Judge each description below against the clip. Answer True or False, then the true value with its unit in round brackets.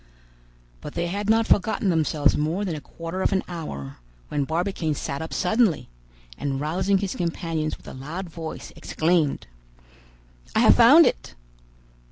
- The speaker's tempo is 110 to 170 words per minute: True (155 wpm)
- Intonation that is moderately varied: True (3.8 semitones)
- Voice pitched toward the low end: False (165 Hz)